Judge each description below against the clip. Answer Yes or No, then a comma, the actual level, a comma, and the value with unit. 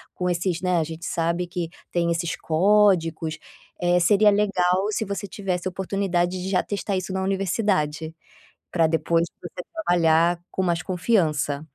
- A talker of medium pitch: Yes, medium, 180 Hz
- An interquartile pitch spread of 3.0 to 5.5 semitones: No, narrow, 2.5 semitones